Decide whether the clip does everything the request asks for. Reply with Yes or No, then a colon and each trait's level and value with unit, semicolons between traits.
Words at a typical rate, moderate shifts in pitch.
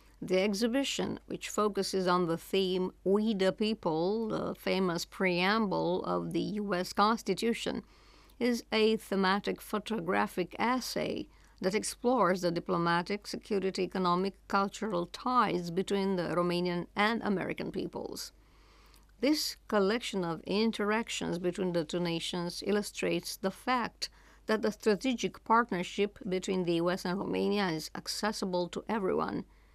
No: slow, 120 wpm; average, 3.3 semitones